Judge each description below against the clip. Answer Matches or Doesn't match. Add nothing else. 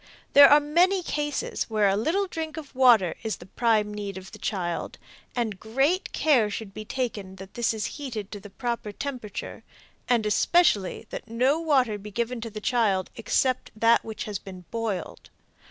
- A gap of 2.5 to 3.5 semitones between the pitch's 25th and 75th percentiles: Doesn't match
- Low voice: Doesn't match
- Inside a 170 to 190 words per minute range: Matches